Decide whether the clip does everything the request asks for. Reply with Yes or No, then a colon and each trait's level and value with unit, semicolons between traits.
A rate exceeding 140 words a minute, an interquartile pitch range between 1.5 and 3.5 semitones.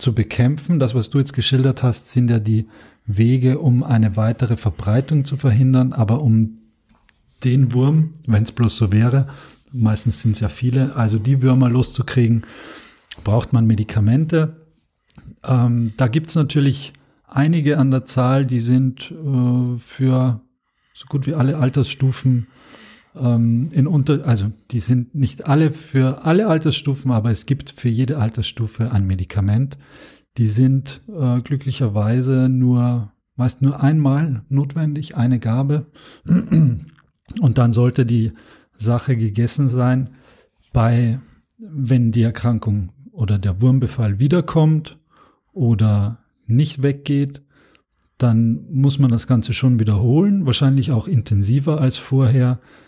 No: average, 130 wpm; average, 3.1 semitones